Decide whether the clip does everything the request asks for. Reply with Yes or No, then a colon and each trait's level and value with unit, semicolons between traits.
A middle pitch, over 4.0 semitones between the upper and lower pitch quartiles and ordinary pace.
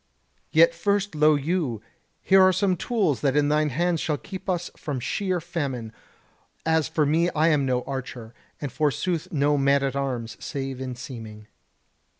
Yes: medium, 150 Hz; average, 4.5 semitones; average, 165 wpm